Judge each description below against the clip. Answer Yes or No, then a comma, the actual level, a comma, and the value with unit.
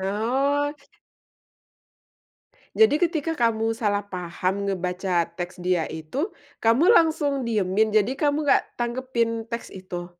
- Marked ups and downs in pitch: Yes, wide, 6.7 semitones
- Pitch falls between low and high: No, high, 225 Hz